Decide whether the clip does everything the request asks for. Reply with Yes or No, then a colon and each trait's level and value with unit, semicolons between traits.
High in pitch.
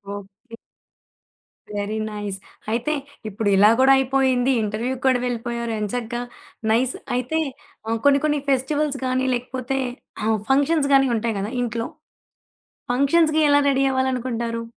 Yes: very high, 250 Hz